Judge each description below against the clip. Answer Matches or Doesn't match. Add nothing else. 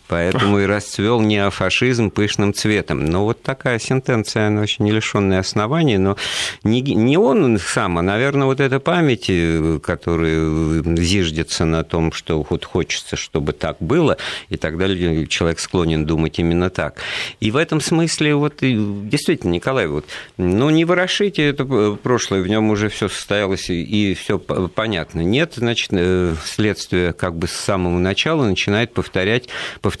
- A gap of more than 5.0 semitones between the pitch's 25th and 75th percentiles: Matches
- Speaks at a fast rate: Doesn't match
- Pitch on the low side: Matches